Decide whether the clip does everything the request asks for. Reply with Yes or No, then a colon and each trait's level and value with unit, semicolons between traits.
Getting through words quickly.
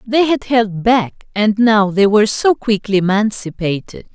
No: average, 160 wpm